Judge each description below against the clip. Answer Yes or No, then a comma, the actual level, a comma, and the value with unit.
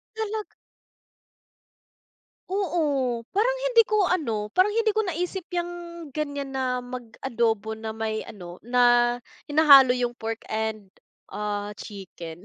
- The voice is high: Yes, very high, 250 Hz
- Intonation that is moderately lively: No, wide, 8.0 semitones